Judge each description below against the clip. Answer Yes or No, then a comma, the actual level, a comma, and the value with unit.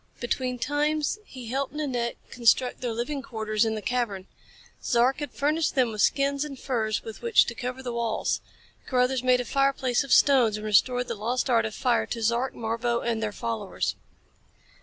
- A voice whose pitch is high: Yes, high, 245 Hz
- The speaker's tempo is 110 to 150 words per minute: No, average, 180 wpm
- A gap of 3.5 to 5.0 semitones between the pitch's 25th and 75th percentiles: No, average, 2.8 semitones